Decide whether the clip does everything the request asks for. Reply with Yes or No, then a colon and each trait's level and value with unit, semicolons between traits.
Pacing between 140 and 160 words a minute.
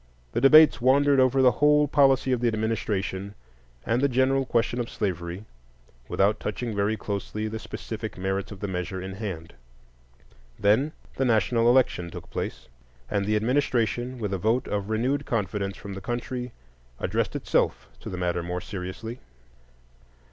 Yes: average, 155 wpm